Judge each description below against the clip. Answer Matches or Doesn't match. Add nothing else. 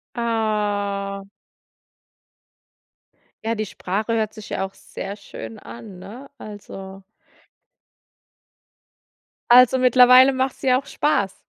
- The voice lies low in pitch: Doesn't match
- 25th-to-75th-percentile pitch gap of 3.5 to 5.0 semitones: Matches